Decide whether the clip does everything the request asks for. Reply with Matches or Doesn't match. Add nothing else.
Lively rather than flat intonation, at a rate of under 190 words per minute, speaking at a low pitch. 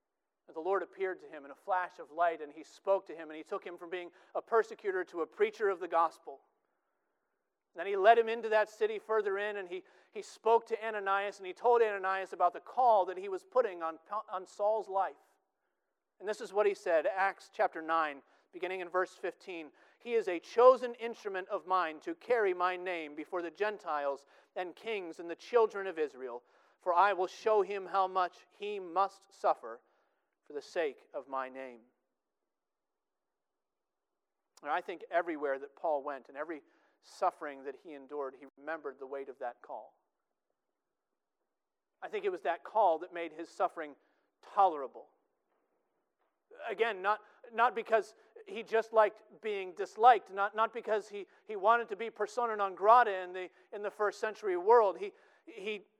Doesn't match